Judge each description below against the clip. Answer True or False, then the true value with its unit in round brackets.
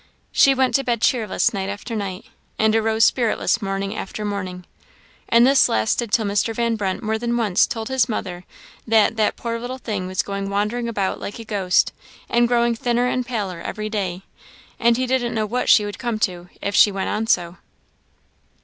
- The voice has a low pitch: False (220 Hz)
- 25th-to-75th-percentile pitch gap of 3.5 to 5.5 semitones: False (3.0 semitones)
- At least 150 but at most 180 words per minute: False (195 wpm)